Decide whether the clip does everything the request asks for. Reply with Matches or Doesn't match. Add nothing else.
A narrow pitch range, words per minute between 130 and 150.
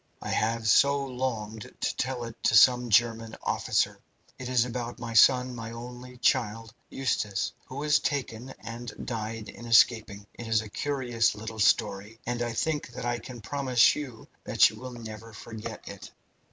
Doesn't match